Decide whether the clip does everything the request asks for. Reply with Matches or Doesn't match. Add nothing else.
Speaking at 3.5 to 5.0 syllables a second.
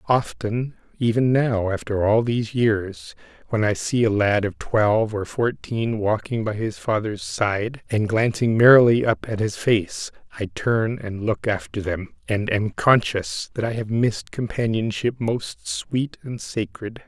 Matches